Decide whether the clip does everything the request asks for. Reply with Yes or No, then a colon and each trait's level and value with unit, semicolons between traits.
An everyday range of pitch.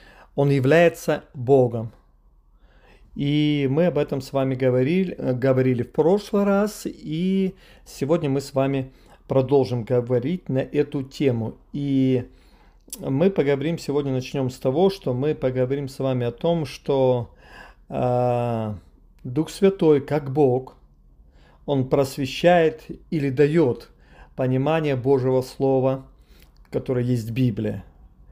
Yes: average, 3.3 semitones